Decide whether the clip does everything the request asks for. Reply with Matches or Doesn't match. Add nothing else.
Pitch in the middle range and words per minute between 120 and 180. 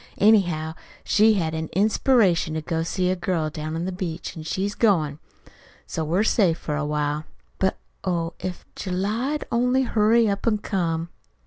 Matches